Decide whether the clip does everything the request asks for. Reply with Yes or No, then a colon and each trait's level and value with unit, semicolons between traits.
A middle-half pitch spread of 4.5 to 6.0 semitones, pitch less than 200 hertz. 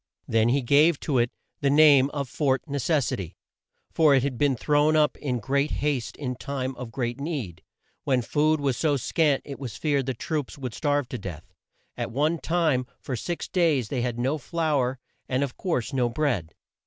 No: average, 3.2 semitones; medium, 140 Hz